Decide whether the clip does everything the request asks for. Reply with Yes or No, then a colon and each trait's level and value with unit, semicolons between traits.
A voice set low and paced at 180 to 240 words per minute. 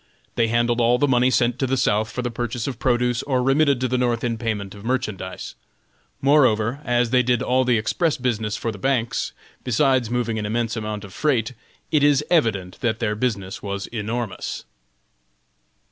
Yes: low, 120 Hz; average, 185 wpm